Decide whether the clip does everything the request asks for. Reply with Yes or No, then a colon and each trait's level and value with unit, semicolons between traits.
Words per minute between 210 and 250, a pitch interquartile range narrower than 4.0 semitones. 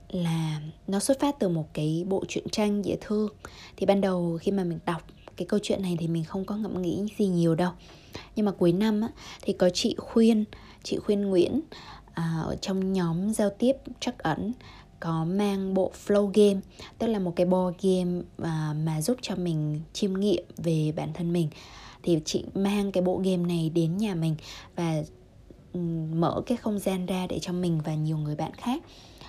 No: average, 195 wpm; average, 3.5 semitones